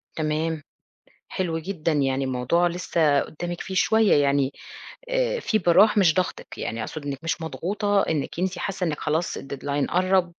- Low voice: No, medium, 165 Hz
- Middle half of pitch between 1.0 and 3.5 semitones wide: No, average, 4.4 semitones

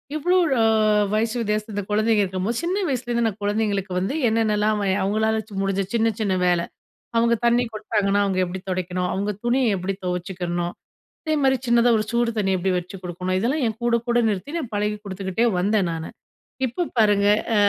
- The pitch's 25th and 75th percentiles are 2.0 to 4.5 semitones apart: Yes, average, 3.6 semitones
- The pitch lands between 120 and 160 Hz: No, high, 210 Hz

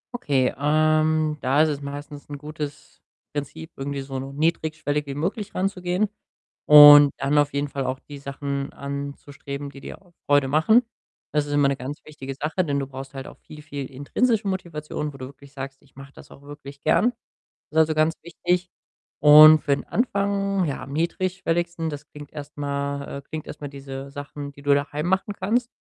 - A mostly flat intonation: Yes, narrow, 2.2 semitones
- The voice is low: No, medium, 145 Hz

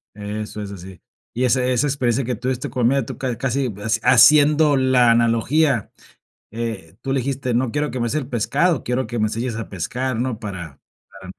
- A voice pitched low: Yes, low, 125 Hz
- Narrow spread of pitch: No, average, 3.0 semitones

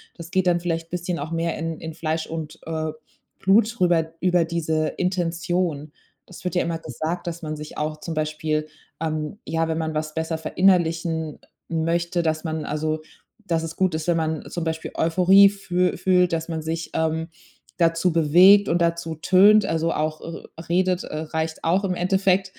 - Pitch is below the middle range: No, medium, 165 Hz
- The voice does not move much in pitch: Yes, narrow, 2.0 semitones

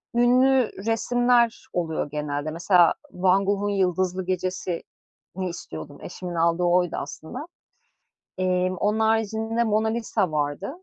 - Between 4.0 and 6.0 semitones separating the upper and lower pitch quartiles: Yes, average, 4.3 semitones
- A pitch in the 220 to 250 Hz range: No, medium, 185 Hz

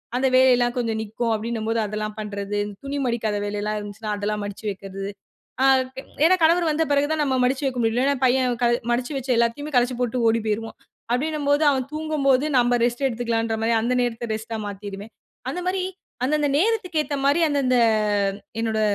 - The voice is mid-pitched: No, high, 240 Hz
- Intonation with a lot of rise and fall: No, average, 4.1 semitones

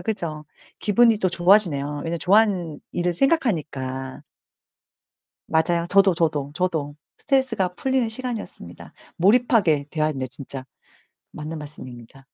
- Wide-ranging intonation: Yes, wide, 6.2 semitones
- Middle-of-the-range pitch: Yes, medium, 170 Hz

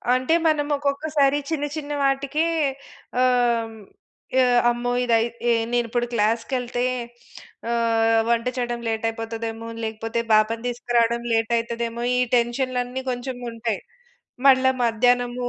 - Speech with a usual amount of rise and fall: No, narrow, 1.9 semitones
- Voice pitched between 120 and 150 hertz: No, high, 240 Hz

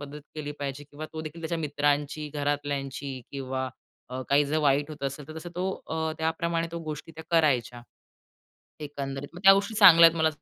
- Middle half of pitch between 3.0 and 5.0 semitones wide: No, narrow, 2.4 semitones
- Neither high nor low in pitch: Yes, medium, 145 Hz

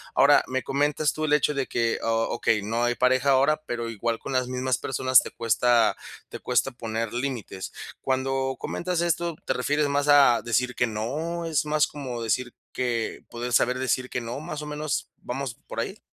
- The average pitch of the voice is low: Yes, low, 130 Hz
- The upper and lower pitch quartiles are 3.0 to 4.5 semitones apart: Yes, average, 3.5 semitones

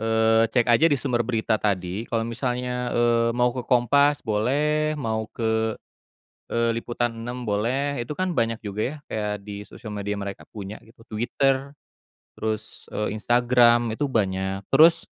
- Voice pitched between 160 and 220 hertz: No, low, 115 Hz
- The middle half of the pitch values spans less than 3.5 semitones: Yes, narrow, 2.5 semitones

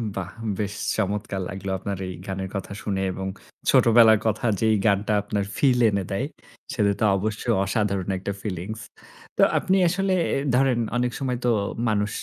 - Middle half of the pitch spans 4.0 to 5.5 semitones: No, average, 3.0 semitones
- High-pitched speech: No, low, 105 Hz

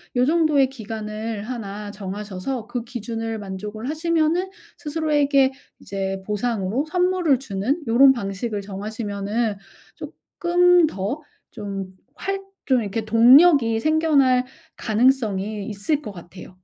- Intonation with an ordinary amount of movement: No, wide, 5.7 semitones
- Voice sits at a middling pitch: No, high, 230 Hz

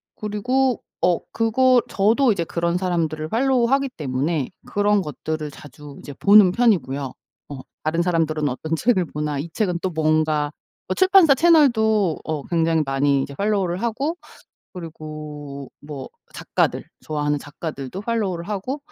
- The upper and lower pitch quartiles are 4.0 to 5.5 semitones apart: No, wide, 6.6 semitones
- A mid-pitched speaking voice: Yes, medium, 170 Hz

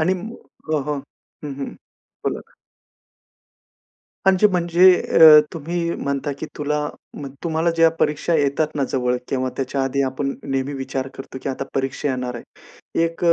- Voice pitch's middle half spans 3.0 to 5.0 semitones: Yes, average, 3.6 semitones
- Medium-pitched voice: Yes, medium, 145 Hz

